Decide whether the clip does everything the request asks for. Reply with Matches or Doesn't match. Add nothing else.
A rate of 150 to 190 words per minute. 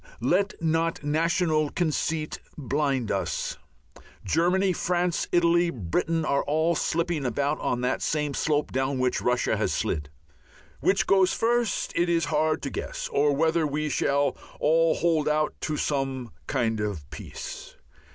Doesn't match